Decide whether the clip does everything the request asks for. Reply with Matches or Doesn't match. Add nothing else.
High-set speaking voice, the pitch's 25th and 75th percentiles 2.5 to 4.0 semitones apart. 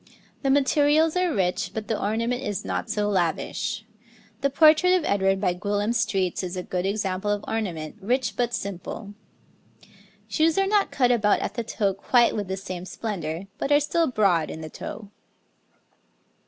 Doesn't match